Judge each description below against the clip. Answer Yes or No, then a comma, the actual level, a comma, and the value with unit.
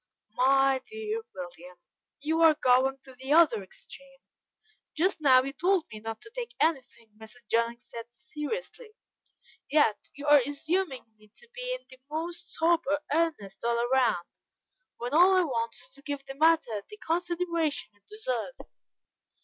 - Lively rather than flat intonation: Yes, wide, 5.9 semitones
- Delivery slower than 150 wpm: No, average, 155 wpm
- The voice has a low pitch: No, very high, 285 Hz